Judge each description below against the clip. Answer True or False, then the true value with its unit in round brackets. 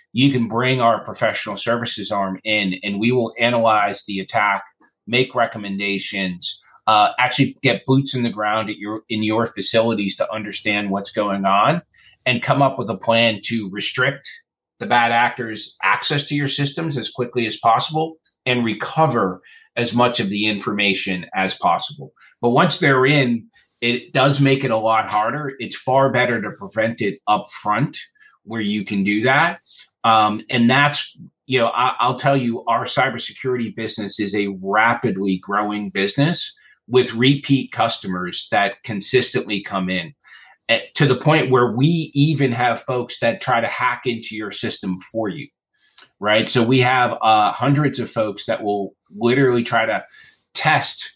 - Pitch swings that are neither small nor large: True (3.7 semitones)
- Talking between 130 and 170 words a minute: True (165 wpm)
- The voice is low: True (115 Hz)